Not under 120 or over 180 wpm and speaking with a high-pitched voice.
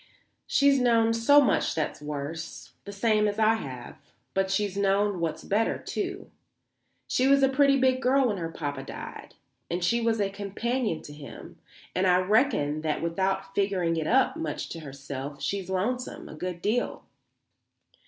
Yes: average, 165 wpm; high, 195 Hz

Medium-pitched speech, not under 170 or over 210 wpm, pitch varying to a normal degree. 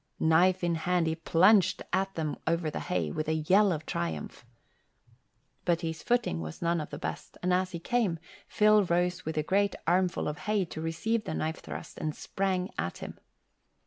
Yes: medium, 170 Hz; average, 190 wpm; average, 3.0 semitones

